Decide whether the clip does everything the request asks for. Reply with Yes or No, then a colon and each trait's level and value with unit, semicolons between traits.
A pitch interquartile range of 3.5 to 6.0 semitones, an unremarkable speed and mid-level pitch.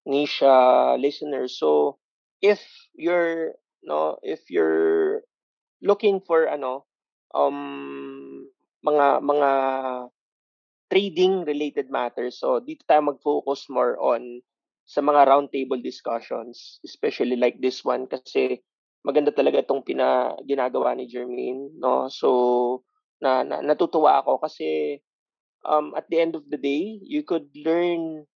Yes: wide, 5.6 semitones; average, 120 wpm; medium, 145 Hz